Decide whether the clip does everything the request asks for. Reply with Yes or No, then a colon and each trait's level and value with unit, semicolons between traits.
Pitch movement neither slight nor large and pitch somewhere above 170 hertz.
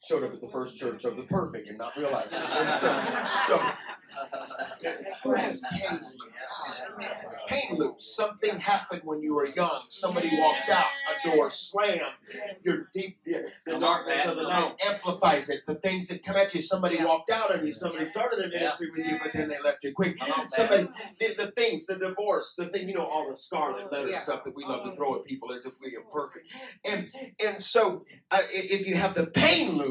Yes: average, 4.3 semitones; high, 190 Hz